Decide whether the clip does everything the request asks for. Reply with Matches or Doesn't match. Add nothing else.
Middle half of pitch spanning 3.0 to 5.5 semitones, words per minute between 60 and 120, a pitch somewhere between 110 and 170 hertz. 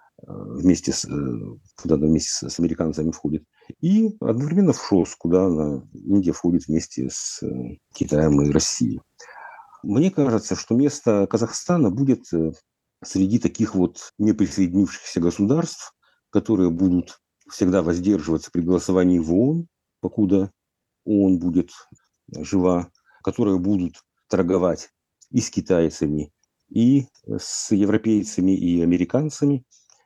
Doesn't match